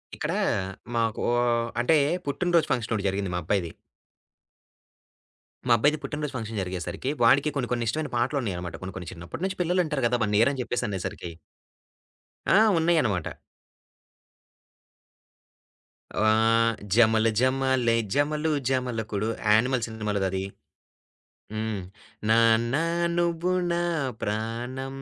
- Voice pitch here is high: No, low, 115 Hz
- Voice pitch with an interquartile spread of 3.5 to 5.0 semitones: Yes, average, 4.5 semitones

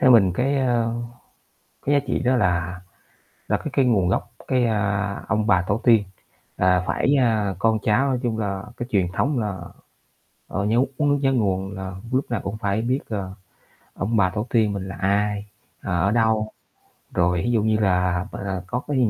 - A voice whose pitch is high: No, low, 105 Hz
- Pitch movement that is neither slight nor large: Yes, average, 3.8 semitones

